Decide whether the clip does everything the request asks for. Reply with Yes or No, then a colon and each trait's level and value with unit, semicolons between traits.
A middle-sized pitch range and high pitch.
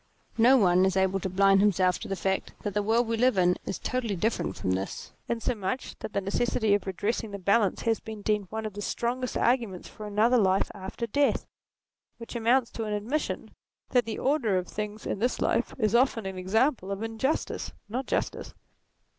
Yes: average, 3.4 semitones; high, 215 Hz